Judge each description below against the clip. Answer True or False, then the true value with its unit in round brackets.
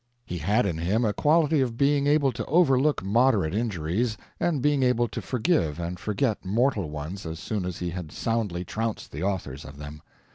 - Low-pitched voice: True (105 Hz)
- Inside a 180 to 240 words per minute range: True (190 wpm)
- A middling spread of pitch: False (7.1 semitones)